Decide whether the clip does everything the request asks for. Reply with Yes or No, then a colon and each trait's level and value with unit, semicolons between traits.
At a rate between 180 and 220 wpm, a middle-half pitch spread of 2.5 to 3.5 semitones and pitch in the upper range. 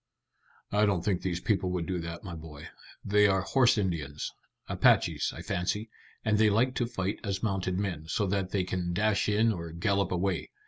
No: average, 190 wpm; average, 3.0 semitones; very low, 95 Hz